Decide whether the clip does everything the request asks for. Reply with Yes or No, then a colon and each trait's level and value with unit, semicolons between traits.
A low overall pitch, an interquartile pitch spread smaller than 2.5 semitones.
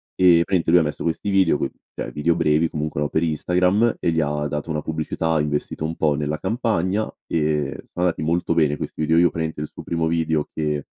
Yes: very low, 80 Hz; narrow, 2.1 semitones